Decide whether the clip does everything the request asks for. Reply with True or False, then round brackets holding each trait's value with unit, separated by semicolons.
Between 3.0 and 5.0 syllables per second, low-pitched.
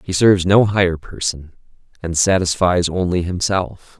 True (4.7 syllables/s; 90 Hz)